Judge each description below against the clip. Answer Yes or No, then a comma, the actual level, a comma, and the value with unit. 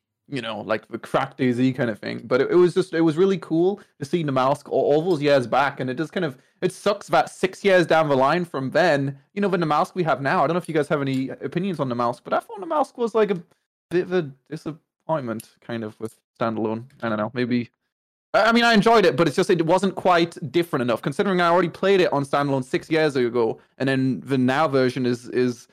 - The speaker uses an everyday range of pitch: No, wide, 5.8 semitones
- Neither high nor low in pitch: Yes, medium, 155 Hz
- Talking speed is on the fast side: Yes, fast, 260 wpm